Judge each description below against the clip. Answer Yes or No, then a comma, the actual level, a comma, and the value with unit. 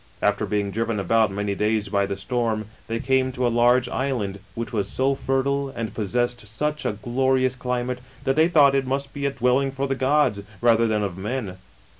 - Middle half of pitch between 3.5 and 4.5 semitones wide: Yes, average, 4.0 semitones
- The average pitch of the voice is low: Yes, low, 120 Hz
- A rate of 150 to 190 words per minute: No, fast, 205 wpm